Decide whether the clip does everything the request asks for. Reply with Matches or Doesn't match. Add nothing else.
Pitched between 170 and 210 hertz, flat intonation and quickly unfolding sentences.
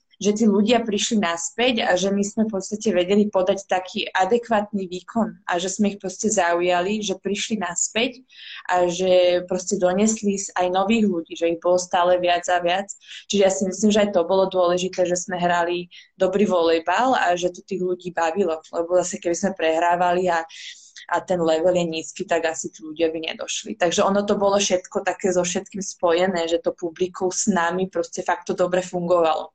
Matches